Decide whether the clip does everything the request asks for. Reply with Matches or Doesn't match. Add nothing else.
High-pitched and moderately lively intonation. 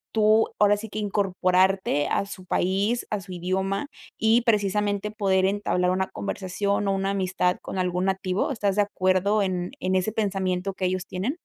Doesn't match